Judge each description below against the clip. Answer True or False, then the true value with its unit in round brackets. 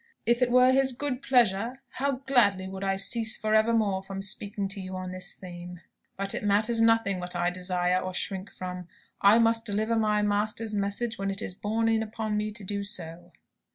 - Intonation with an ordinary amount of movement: True (3.1 semitones)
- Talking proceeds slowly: False (200 wpm)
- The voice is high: True (205 Hz)